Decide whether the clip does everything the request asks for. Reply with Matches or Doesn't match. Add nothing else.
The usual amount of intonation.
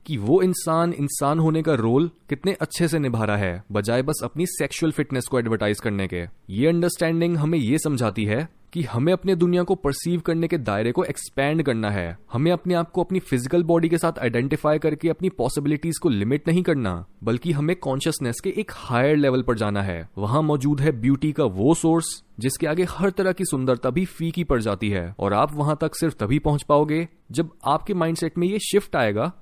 Doesn't match